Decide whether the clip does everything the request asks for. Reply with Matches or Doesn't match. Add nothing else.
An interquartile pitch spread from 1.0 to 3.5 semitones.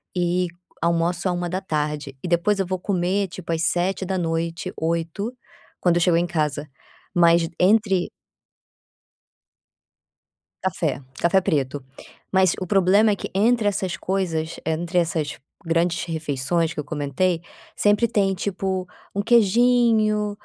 Matches